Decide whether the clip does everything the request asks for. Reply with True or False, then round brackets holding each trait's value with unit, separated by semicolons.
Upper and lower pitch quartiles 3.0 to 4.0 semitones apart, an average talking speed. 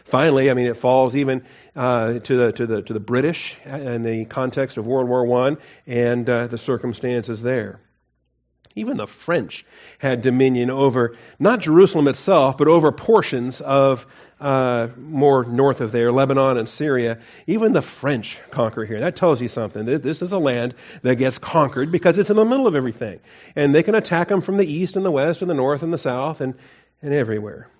True (3.7 semitones; 195 wpm)